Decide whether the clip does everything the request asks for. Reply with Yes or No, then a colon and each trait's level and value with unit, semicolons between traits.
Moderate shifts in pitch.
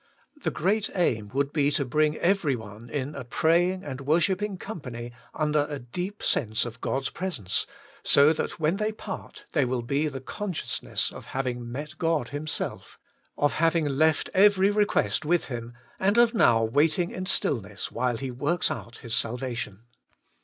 No: wide, 6.3 semitones